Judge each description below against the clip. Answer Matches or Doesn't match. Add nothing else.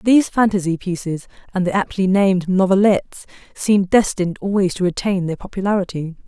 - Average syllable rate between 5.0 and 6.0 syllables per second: Matches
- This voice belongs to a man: Doesn't match